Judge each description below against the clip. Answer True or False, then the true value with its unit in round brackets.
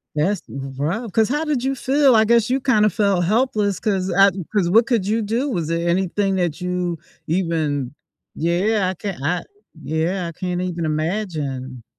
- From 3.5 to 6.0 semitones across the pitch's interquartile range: True (4.6 semitones)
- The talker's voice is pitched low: False (185 Hz)